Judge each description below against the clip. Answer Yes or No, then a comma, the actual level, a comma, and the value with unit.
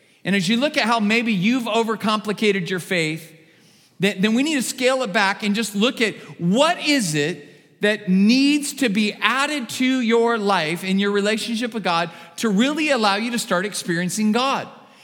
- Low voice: No, high, 215 Hz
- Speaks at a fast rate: No, average, 185 wpm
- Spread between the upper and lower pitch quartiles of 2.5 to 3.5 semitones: No, average, 4.1 semitones